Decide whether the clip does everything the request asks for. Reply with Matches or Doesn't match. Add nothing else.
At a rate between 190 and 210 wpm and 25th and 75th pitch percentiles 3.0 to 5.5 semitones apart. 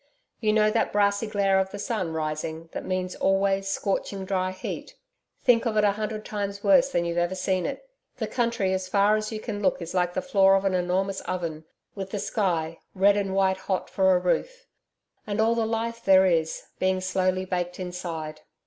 Doesn't match